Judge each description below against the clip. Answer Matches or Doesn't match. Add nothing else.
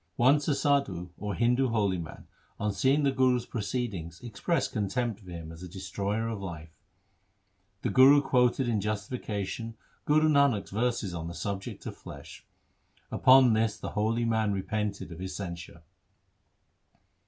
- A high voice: Doesn't match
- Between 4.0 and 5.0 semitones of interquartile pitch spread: Matches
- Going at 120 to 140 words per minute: Doesn't match